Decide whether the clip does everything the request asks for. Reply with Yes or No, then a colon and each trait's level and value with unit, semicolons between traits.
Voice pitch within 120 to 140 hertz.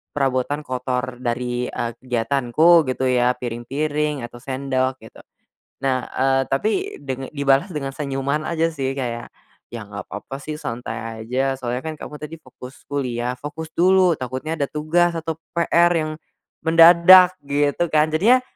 Yes: low, 135 Hz